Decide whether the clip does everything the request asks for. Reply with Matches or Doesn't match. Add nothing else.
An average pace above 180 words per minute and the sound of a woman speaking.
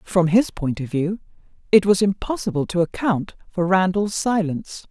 Doesn't match